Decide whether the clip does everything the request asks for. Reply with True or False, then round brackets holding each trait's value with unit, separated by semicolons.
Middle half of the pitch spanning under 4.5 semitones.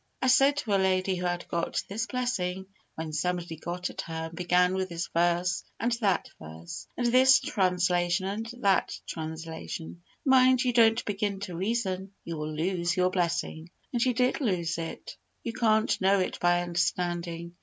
True (4.1 semitones)